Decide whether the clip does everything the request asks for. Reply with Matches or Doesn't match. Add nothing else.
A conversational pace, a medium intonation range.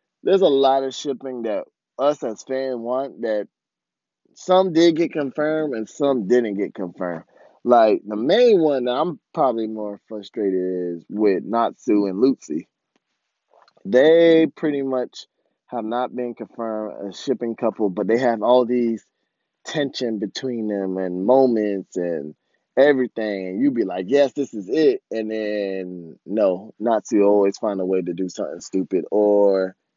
Matches